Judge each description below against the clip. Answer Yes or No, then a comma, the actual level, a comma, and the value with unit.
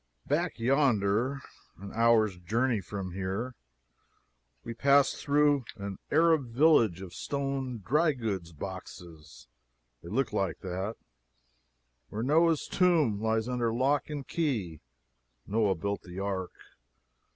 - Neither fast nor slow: No, slow, 120 wpm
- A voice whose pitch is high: No, low, 115 Hz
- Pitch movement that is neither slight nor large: No, wide, 6.3 semitones